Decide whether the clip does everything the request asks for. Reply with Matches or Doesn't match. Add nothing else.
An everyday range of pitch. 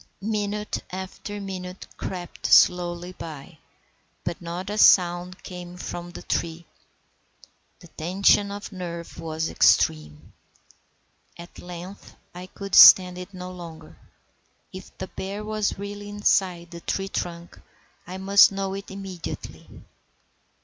Doesn't match